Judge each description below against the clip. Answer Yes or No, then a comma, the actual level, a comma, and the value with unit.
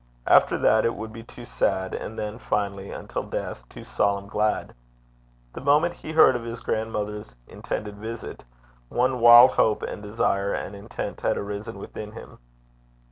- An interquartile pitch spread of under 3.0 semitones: Yes, narrow, 2.5 semitones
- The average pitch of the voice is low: Yes, low, 110 Hz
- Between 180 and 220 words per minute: No, average, 160 wpm